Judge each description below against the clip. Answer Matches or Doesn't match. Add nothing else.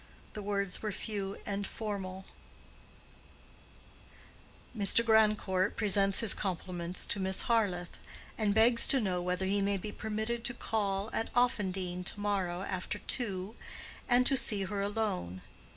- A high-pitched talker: Matches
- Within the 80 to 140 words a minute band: Matches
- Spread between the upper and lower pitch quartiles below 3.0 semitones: Matches